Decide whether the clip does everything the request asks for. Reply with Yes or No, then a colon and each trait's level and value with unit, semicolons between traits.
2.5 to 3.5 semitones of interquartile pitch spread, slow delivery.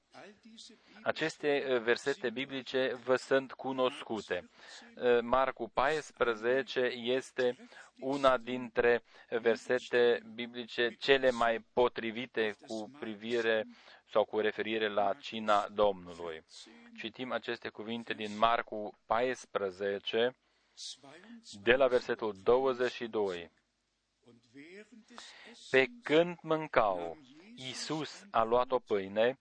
Yes: average, 2.8 semitones; slow, 85 wpm